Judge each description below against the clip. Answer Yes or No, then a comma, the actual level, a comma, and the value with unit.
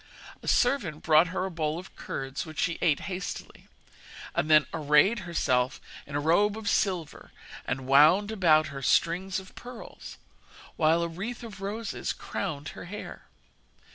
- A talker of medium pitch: Yes, medium, 170 Hz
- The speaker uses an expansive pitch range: No, average, 4.4 semitones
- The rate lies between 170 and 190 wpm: No, average, 155 wpm